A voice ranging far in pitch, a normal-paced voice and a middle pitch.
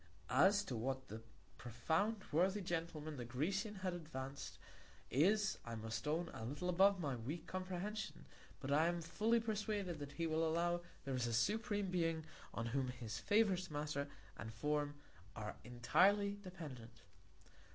Yes: wide, 6.4 semitones; average, 150 wpm; medium, 160 Hz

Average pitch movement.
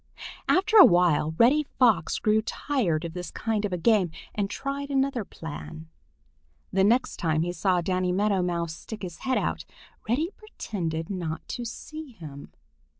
No: wide, 6.6 semitones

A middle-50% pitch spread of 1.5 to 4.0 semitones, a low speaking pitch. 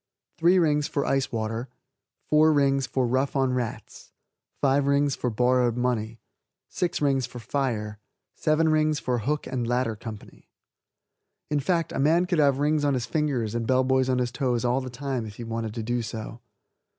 Yes: average, 3.4 semitones; low, 130 Hz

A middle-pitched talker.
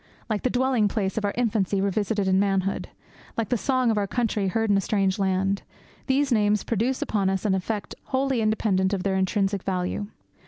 No: high, 205 Hz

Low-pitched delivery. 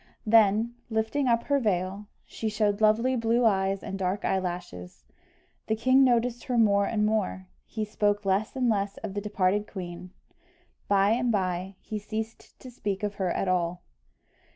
No: high, 210 Hz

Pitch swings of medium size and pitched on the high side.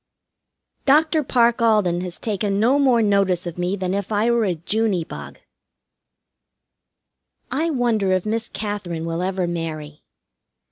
Yes: average, 4.5 semitones; high, 200 Hz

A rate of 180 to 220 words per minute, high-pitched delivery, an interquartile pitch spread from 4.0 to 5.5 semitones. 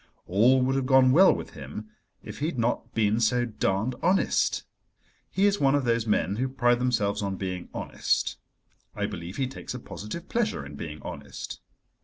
No: average, 185 wpm; low, 120 Hz; average, 4.6 semitones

